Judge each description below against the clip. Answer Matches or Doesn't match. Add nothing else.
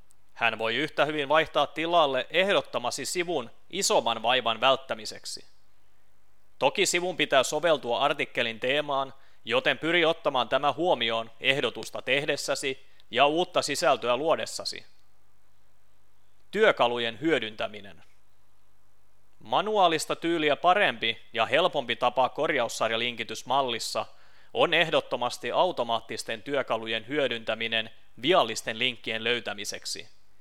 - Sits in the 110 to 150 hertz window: Matches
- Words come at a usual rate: Doesn't match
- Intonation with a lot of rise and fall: Matches